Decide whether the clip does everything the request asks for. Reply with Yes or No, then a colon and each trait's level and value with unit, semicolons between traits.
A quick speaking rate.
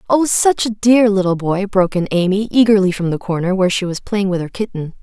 Yes: fast, 240 wpm